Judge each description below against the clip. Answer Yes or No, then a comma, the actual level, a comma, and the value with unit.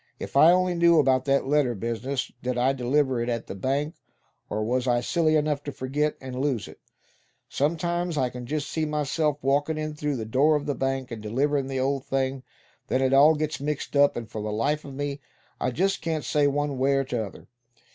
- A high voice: No, medium, 140 Hz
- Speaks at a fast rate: Yes, fast, 215 wpm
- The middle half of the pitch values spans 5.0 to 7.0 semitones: No, average, 2.8 semitones